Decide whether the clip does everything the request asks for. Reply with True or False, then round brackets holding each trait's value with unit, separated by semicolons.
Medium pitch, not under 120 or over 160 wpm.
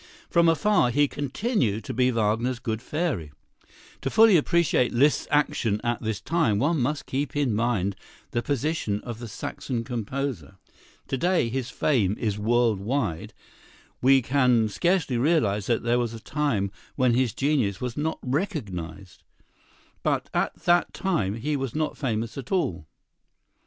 False (125 Hz; 150 wpm)